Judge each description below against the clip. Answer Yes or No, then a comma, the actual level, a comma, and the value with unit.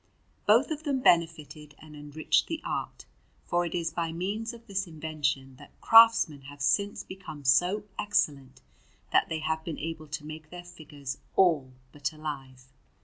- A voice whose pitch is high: No, medium, 160 Hz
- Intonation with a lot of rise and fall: No, average, 4.2 semitones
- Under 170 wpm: Yes, average, 160 wpm